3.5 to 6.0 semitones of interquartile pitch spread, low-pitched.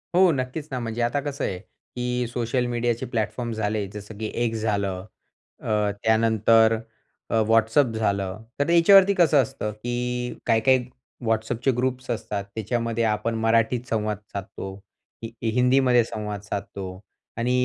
No: narrow, 2.4 semitones; low, 115 Hz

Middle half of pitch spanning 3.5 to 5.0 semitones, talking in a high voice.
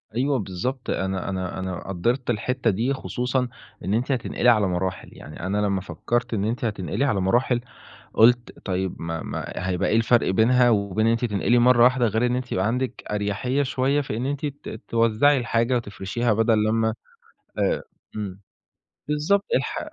No: average, 4.2 semitones; low, 115 Hz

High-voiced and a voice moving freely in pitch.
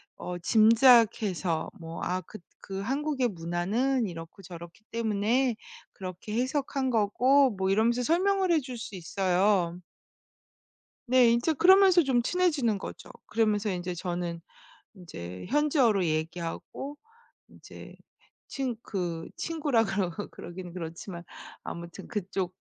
Yes: high, 210 Hz; wide, 6.4 semitones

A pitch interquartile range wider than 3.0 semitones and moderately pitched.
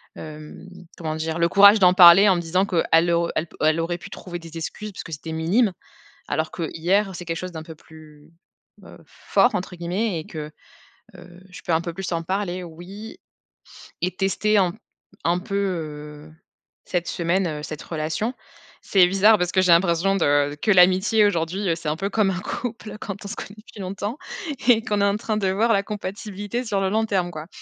Yes: average, 3.5 semitones; medium, 180 Hz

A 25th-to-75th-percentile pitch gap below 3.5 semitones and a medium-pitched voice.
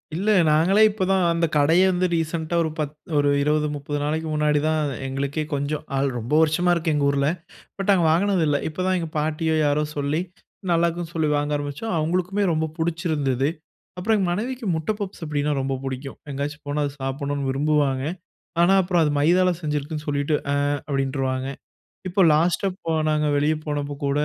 Yes: average, 3.0 semitones; medium, 155 Hz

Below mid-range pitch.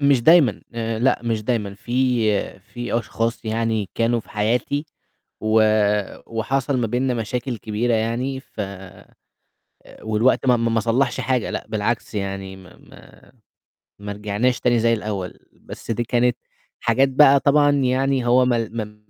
Yes: low, 115 Hz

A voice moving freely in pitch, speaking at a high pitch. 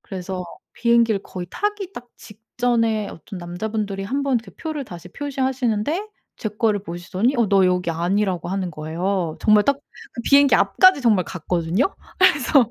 Yes: wide, 5.7 semitones; high, 215 Hz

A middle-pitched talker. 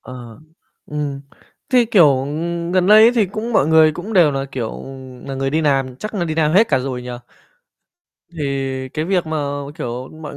Yes: medium, 155 Hz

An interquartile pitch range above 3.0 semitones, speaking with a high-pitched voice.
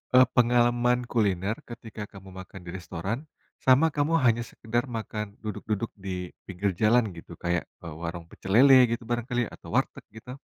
No: average, 4.3 semitones; low, 110 Hz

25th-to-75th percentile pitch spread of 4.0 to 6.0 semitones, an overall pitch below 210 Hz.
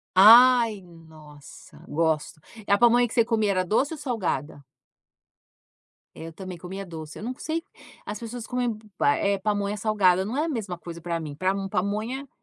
Yes: wide, 5.4 semitones; high, 200 Hz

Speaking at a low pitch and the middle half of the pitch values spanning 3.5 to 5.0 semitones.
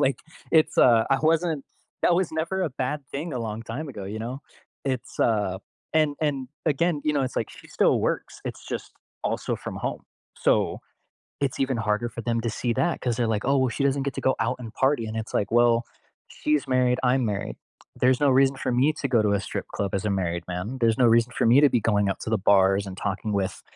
Yes: low, 125 Hz; average, 4.1 semitones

